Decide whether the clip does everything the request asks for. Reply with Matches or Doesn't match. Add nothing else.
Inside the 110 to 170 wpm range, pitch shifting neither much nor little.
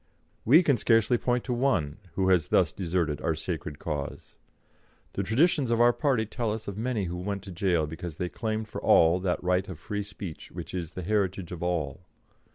Doesn't match